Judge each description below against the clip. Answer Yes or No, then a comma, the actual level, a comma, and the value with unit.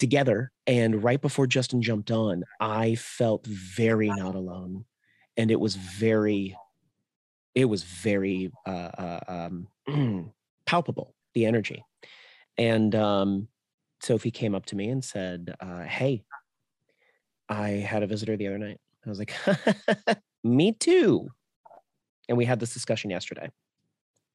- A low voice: Yes, low, 110 Hz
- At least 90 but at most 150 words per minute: Yes, slow, 135 wpm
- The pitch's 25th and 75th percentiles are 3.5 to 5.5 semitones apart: Yes, average, 4.0 semitones